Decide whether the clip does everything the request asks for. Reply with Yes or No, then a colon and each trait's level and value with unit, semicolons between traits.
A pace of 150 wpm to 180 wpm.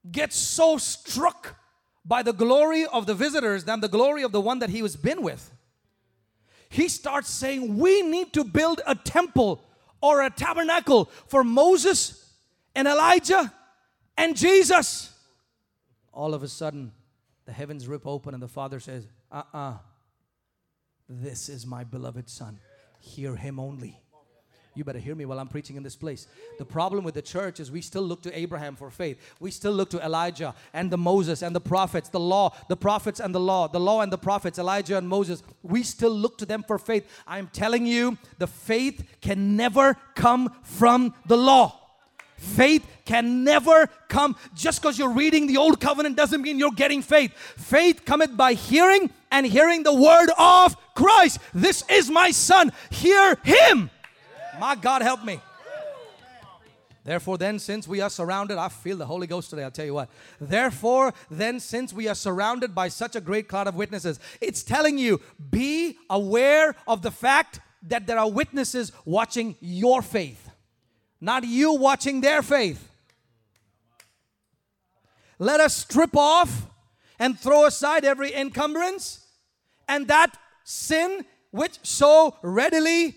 Yes: average, 165 wpm